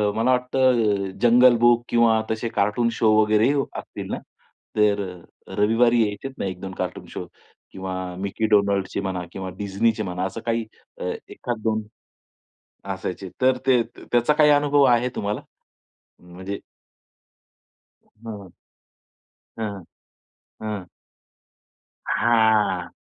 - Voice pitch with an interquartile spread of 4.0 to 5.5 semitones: No, average, 3.1 semitones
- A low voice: Yes, low, 110 Hz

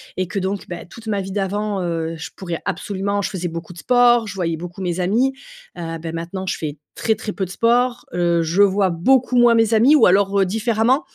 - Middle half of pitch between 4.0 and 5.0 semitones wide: Yes, average, 4.3 semitones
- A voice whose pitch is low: No, high, 195 Hz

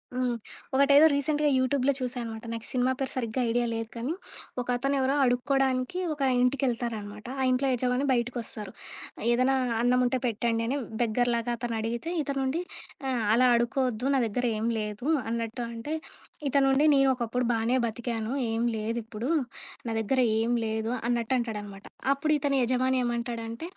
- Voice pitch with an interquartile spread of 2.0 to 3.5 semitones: Yes, narrow, 2.5 semitones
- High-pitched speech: Yes, high, 245 Hz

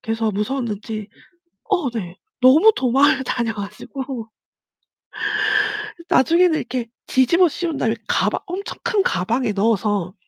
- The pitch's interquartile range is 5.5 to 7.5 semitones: No, average, 5.1 semitones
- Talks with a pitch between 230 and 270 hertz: Yes, high, 240 Hz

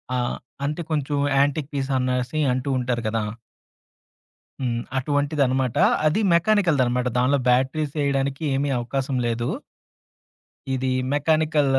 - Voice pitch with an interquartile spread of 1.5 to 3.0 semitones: Yes, narrow, 2.6 semitones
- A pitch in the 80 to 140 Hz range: Yes, low, 135 Hz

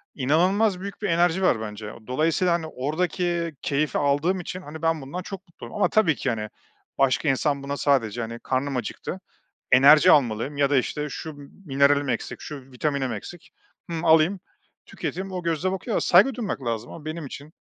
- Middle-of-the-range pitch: Yes, medium, 150 Hz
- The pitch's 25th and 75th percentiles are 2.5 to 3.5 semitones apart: No, average, 4.6 semitones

